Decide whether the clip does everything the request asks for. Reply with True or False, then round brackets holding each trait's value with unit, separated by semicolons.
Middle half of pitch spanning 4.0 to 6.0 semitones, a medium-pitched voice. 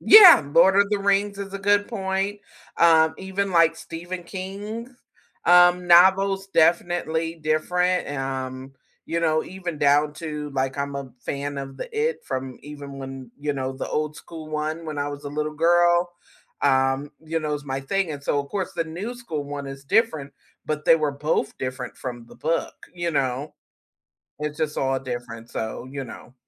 True (4.3 semitones; 155 Hz)